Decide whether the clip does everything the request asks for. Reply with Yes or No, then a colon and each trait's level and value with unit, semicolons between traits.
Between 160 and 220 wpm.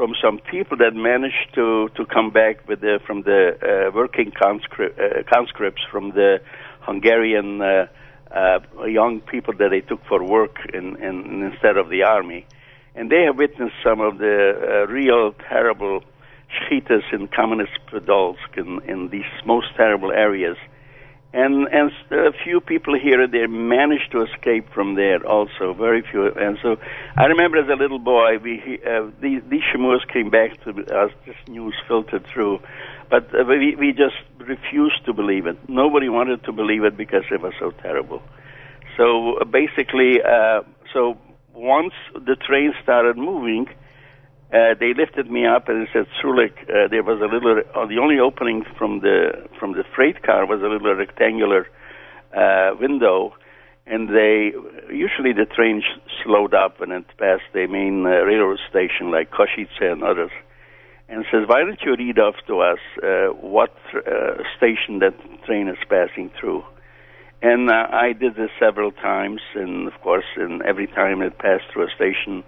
Yes: average, 170 wpm